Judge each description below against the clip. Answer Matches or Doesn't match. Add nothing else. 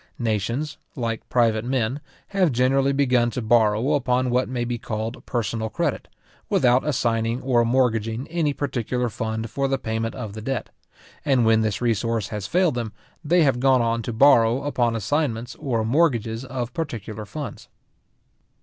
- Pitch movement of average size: Matches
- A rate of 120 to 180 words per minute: Matches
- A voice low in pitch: Matches